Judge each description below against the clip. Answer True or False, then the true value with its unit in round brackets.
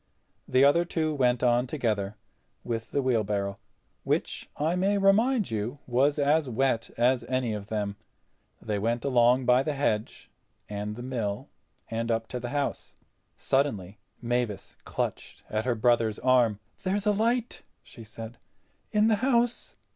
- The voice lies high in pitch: False (125 Hz)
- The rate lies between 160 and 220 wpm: False (145 wpm)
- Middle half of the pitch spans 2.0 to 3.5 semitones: False (4.7 semitones)